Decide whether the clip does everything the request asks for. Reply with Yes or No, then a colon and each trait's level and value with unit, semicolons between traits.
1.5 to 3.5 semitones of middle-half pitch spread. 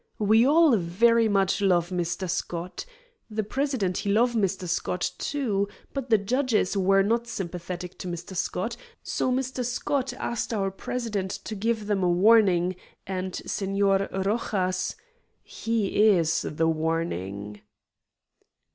No: average, 4.2 semitones